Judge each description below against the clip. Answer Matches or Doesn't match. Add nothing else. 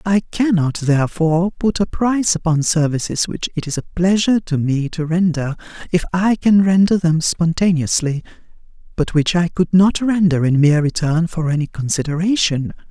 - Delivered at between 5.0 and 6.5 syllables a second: Matches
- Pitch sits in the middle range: Matches